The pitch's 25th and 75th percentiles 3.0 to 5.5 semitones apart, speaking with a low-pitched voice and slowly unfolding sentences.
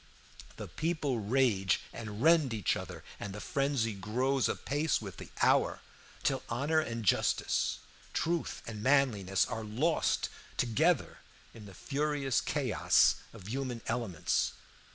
Yes: average, 4.9 semitones; low, 120 Hz; slow, 130 wpm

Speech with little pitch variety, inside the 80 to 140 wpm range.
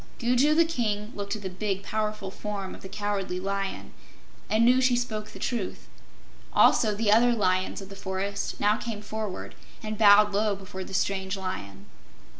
No: narrow, 2.1 semitones; average, 175 wpm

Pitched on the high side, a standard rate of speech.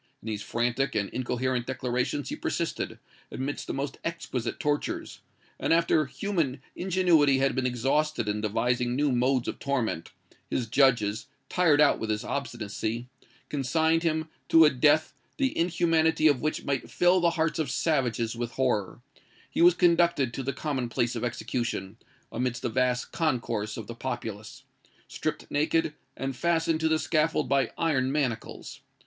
No: low, 135 Hz; average, 155 wpm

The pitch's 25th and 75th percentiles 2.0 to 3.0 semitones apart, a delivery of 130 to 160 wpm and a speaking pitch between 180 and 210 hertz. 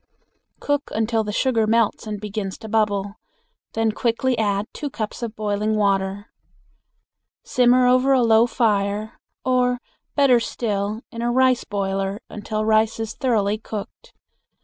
No: narrow, 2.6 semitones; average, 140 wpm; high, 220 Hz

